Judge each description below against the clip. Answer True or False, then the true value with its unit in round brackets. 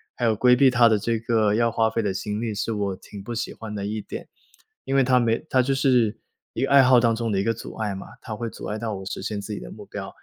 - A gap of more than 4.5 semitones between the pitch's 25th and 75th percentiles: False (2.5 semitones)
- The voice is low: True (115 Hz)